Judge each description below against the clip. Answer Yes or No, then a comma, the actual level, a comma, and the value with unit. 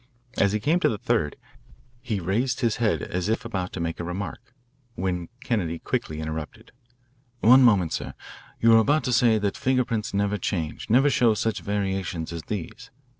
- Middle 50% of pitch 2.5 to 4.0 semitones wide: No, average, 4.8 semitones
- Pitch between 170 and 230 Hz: No, low, 105 Hz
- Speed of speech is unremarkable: Yes, average, 180 wpm